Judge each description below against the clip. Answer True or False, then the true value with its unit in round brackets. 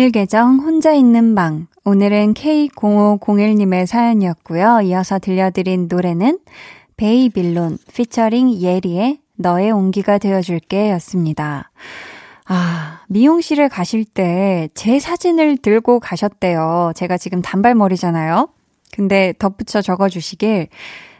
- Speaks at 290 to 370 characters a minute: False (260 characters per minute)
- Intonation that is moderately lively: True (4.3 semitones)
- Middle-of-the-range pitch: False (200 Hz)